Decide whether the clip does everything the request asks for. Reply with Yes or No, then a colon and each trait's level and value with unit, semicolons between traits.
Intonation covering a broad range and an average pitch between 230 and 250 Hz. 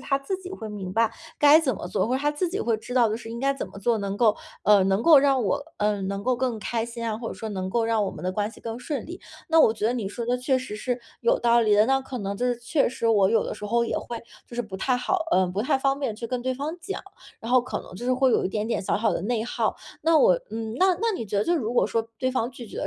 No: average, 3.9 semitones; high, 235 Hz